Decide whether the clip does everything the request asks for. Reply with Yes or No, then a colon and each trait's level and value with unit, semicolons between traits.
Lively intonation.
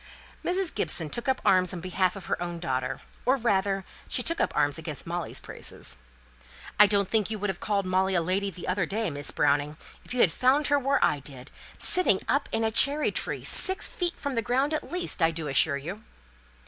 Yes: wide, 7.2 semitones